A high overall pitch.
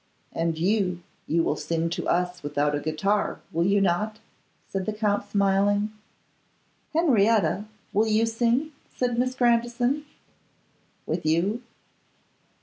Yes: high, 205 Hz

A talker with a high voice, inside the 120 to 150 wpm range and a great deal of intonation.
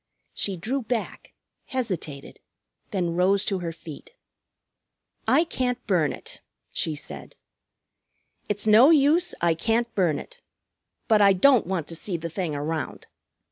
Yes: high, 195 Hz; average, 140 wpm; wide, 6.4 semitones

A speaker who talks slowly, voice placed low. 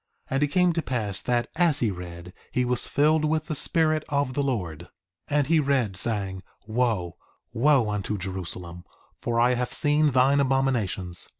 No: average, 180 wpm; low, 125 Hz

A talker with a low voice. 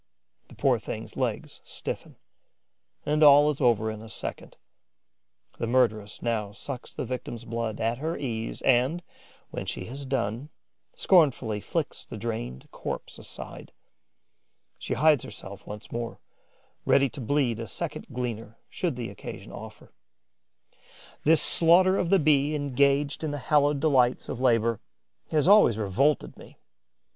Yes: low, 125 Hz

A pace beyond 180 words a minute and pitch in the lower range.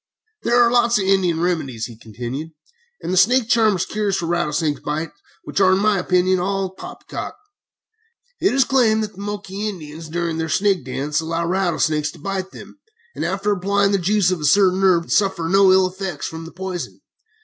No: average, 190 wpm; medium, 185 Hz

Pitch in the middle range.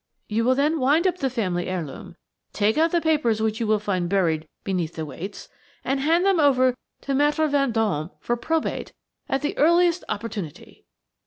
No: high, 240 Hz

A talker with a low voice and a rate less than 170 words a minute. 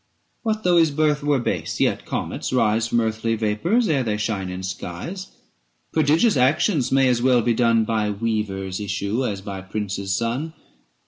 No: low, 115 Hz; average, 175 wpm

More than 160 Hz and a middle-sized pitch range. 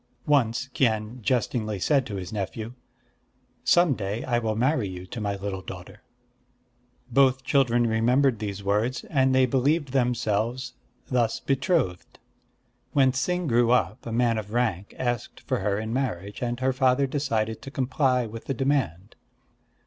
No: low, 120 Hz; average, 3.6 semitones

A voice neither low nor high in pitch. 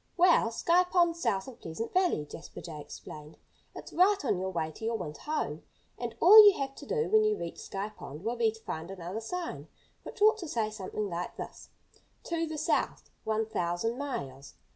No: high, 225 Hz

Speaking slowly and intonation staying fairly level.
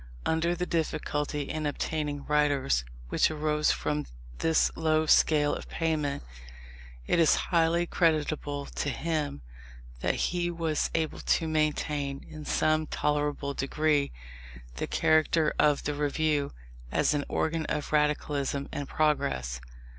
Yes: slow, 125 wpm; narrow, 1.6 semitones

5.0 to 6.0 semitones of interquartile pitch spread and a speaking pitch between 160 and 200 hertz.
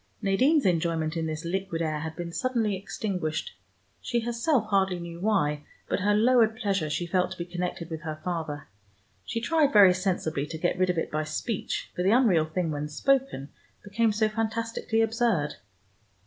Yes: wide, 5.5 semitones; medium, 185 Hz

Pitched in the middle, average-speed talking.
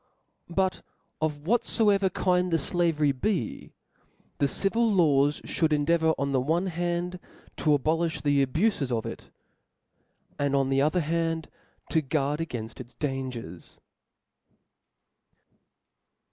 No: medium, 160 Hz; slow, 130 wpm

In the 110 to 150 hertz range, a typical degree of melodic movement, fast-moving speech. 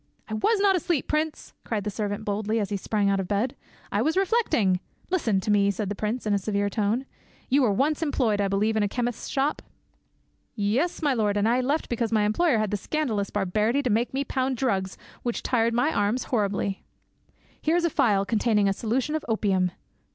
No: high, 220 Hz; average, 4.6 semitones; fast, 210 wpm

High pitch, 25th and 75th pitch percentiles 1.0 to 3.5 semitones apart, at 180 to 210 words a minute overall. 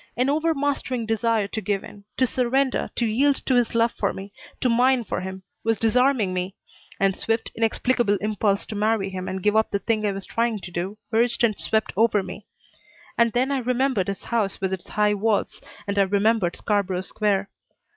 Yes: high, 220 Hz; average, 3.2 semitones; average, 195 wpm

